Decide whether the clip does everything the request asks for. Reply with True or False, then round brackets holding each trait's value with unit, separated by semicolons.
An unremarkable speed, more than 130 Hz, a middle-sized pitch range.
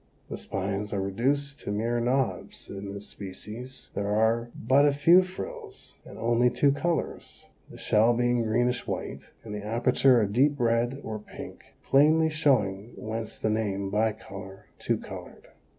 False (155 wpm; 115 Hz; 4.6 semitones)